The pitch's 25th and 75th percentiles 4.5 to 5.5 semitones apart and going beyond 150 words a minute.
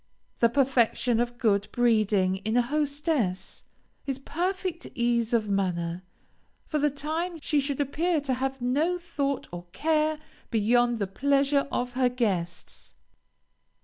No: average, 4.9 semitones; slow, 135 wpm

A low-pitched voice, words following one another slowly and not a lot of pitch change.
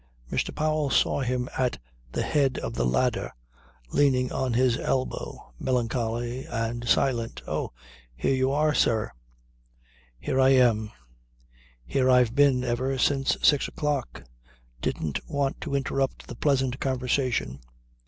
Yes: low, 130 Hz; slow, 130 wpm; narrow, 2.3 semitones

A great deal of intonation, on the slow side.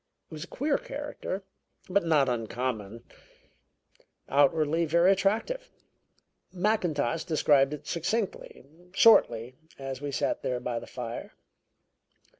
Yes: wide, 6.9 semitones; slow, 110 wpm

